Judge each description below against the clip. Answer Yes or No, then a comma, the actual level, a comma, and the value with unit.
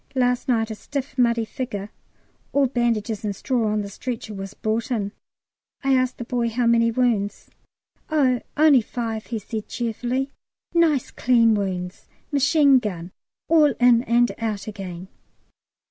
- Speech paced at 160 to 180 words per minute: No, average, 145 wpm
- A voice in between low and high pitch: No, high, 235 Hz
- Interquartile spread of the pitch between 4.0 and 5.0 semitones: No, average, 3.2 semitones